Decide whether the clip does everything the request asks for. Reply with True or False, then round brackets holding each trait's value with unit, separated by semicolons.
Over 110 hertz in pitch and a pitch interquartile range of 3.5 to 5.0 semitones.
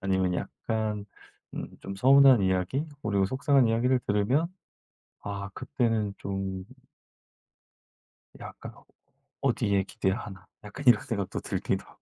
False (105 Hz; 4.1 semitones)